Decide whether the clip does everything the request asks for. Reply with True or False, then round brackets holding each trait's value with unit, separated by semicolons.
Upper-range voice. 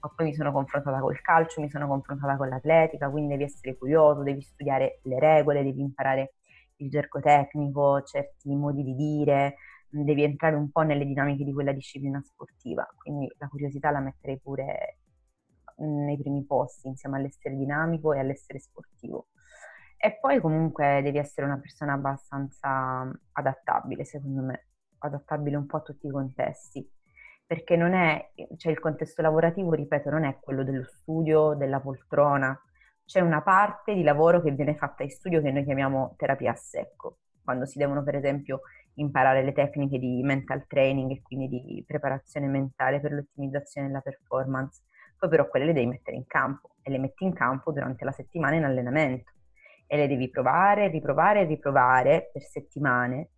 False (140 Hz)